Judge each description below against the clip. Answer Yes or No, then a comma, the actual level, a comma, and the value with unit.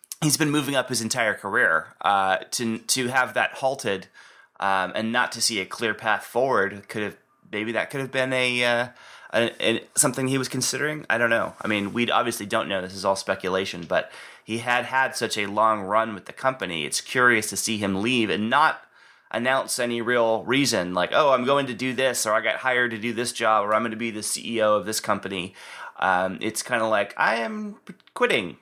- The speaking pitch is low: Yes, low, 115 Hz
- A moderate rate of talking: No, fast, 220 wpm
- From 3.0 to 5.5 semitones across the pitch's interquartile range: Yes, average, 3.4 semitones